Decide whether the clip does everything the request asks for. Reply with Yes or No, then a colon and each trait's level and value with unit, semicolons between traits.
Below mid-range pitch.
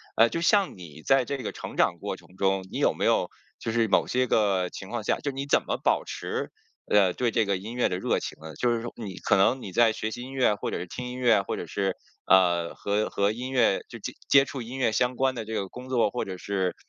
Yes: low, 110 Hz